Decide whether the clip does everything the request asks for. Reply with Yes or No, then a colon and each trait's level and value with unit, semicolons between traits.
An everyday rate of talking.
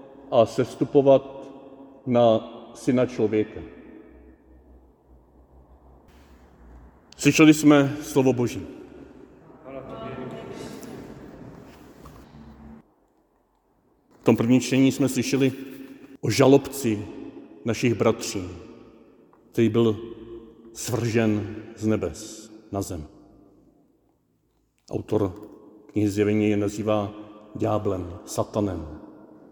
No: slow, 65 wpm